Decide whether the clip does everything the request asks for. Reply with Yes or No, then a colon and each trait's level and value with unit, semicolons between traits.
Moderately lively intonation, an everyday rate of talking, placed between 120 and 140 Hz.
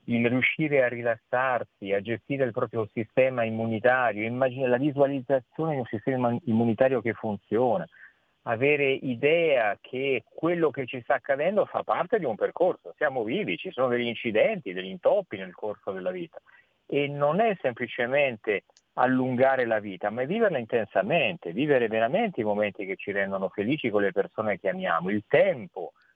Yes: average, 3.7 semitones; average, 160 wpm; low, 125 Hz